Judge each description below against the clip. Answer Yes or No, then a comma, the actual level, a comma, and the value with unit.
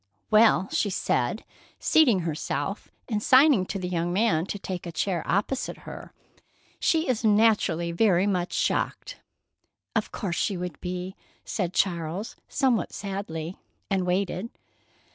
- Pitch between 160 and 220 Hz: Yes, high, 190 Hz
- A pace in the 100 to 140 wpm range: Yes, slow, 135 wpm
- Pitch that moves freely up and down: No, average, 3.5 semitones